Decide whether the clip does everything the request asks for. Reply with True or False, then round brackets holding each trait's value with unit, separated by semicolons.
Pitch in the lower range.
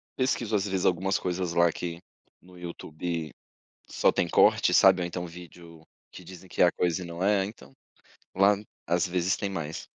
True (90 Hz)